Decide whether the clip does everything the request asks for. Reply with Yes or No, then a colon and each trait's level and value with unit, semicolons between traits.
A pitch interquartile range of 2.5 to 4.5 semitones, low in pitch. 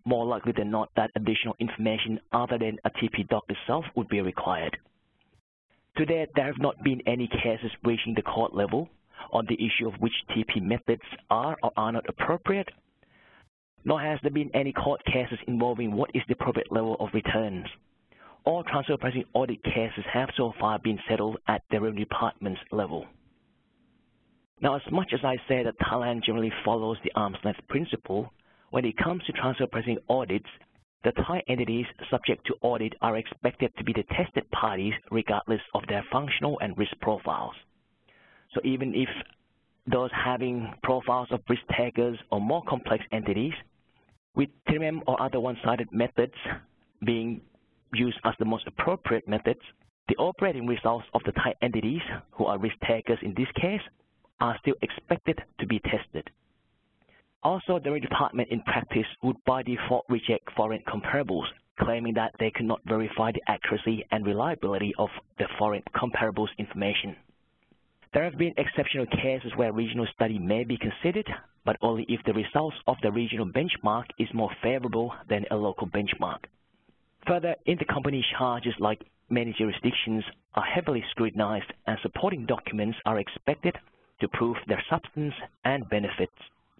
Yes: average, 2.8 semitones; low, 115 Hz